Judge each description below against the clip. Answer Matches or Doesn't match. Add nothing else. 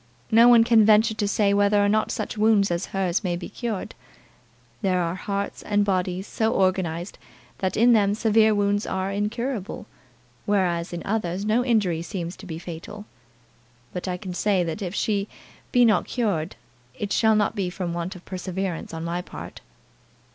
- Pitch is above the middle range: Matches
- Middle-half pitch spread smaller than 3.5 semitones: Matches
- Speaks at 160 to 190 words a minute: Matches